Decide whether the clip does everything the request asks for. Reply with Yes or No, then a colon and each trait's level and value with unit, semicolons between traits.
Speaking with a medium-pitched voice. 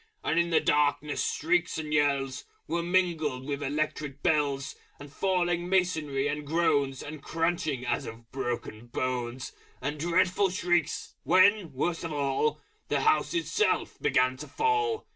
Yes: medium, 150 Hz